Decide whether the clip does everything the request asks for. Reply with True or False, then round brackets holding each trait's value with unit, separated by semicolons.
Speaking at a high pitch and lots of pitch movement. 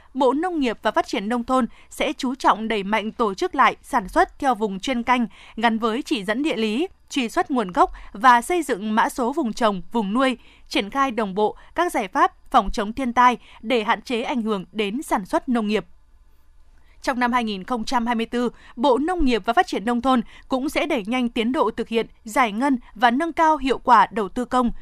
False (245 Hz; 3.8 semitones)